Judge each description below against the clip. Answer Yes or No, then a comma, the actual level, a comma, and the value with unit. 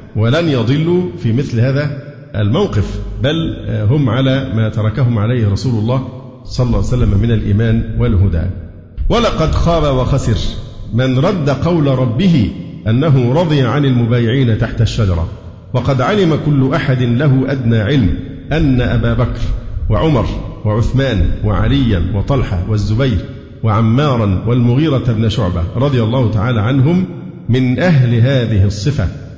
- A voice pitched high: No, low, 120 Hz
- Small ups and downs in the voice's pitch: No, average, 4.0 semitones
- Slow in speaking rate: No, average, 125 wpm